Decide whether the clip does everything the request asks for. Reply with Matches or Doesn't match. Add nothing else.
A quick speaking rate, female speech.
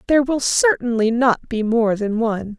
Doesn't match